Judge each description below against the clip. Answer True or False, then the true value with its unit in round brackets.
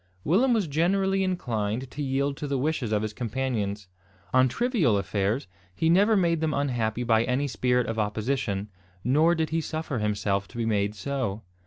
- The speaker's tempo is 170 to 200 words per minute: True (175 wpm)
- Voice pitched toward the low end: True (130 Hz)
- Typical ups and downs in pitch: False (6.7 semitones)